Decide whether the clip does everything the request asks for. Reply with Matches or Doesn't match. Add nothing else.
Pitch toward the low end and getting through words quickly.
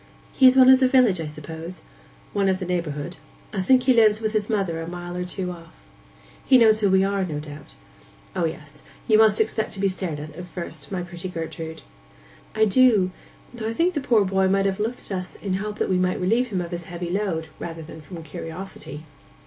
Doesn't match